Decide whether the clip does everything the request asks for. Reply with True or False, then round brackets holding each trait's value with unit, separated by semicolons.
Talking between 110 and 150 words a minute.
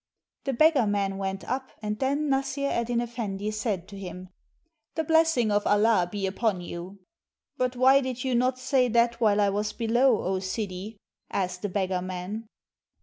False (175 wpm)